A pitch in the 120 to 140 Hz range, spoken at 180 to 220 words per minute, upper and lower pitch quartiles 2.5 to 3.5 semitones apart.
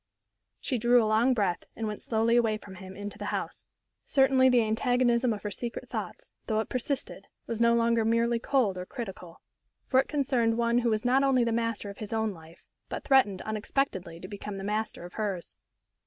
No: high, 225 Hz; average, 200 wpm; average, 3.0 semitones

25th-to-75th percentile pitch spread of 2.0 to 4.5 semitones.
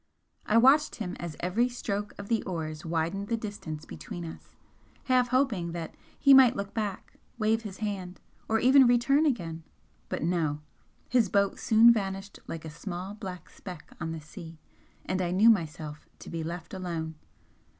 No: average, 5.2 semitones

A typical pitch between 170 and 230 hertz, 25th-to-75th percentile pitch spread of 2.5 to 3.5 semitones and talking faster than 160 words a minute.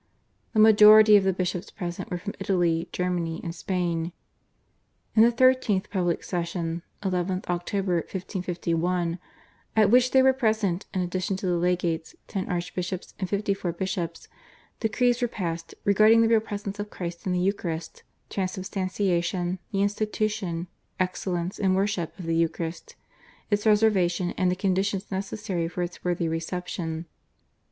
No: medium, 185 Hz; average, 2.9 semitones; average, 145 wpm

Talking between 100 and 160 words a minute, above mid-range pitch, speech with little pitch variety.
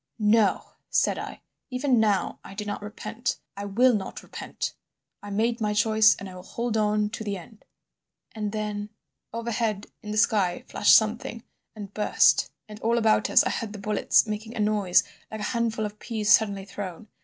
No: average, 185 wpm; high, 215 Hz; narrow, 1.6 semitones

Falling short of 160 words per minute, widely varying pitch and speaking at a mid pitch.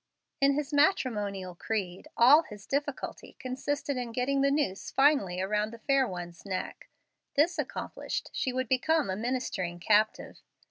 No: average, 145 wpm; wide, 5.9 semitones; very high, 250 Hz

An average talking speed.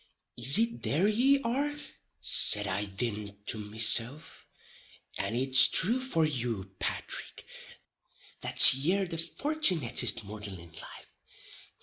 No: slow, 115 wpm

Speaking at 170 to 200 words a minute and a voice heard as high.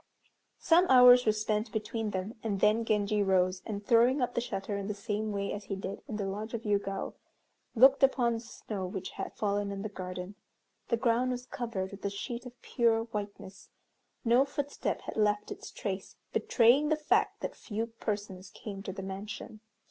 Yes: average, 190 wpm; high, 210 Hz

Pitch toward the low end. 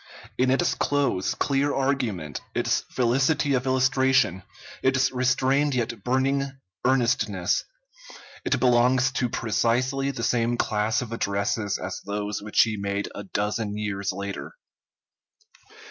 Yes: low, 120 Hz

